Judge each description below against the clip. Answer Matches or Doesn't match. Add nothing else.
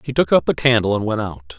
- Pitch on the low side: Matches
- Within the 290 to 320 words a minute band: Matches